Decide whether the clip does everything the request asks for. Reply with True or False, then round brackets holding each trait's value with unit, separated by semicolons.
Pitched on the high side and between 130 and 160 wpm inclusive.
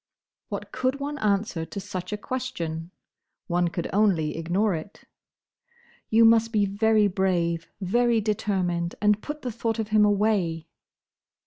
True (205 Hz; 140 wpm)